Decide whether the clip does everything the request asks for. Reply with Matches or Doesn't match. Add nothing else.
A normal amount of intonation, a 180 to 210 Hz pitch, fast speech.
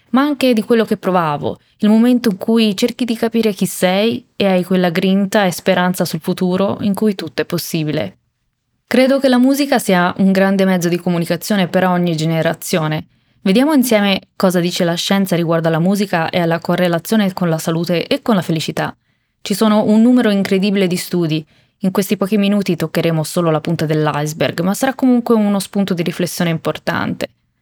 Matches